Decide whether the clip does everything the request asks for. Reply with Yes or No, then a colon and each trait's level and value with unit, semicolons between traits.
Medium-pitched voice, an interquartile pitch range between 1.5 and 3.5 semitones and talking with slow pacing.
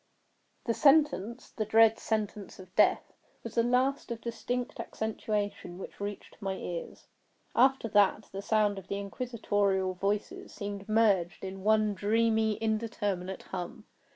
No: high, 210 Hz; narrow, 2.6 semitones; slow, 125 wpm